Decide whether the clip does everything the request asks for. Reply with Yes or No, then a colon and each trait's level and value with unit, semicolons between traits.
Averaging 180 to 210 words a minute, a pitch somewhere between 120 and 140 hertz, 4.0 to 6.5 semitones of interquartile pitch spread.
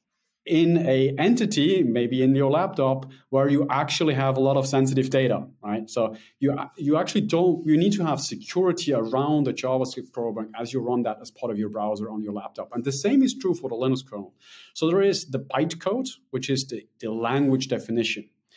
Yes: fast, 205 wpm; low, 135 Hz; average, 5.2 semitones